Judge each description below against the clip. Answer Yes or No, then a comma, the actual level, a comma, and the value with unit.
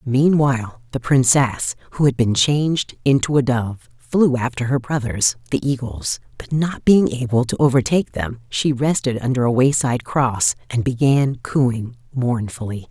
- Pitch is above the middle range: No, low, 125 Hz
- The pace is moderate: Yes, average, 155 wpm